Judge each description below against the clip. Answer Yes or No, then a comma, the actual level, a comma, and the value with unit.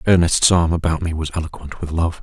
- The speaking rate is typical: No, fast, 215 wpm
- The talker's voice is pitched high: No, very low, 80 Hz